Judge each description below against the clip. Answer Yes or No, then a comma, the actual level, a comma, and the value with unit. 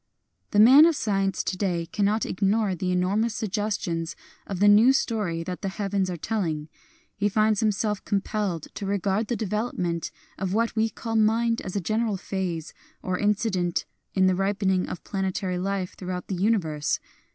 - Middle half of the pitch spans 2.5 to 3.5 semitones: Yes, average, 2.9 semitones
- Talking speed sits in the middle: Yes, average, 165 wpm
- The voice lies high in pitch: Yes, high, 195 Hz